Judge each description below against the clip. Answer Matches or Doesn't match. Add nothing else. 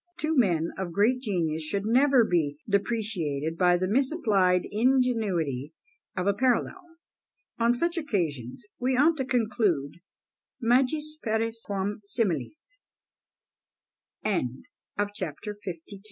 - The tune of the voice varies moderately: Doesn't match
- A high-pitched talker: Matches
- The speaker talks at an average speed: Doesn't match